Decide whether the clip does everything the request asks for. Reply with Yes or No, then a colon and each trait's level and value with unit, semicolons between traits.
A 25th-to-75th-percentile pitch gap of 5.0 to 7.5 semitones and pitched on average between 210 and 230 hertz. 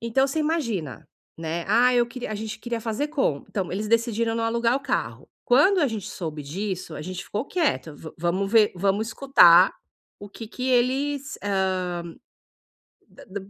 Yes: average, 5.3 semitones; high, 220 Hz